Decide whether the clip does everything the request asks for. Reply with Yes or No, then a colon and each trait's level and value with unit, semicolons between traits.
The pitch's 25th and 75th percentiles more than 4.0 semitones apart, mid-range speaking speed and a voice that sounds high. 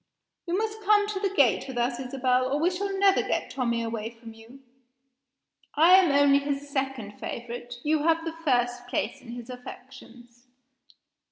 Yes: average, 5.3 semitones; average, 170 wpm; very high, 265 Hz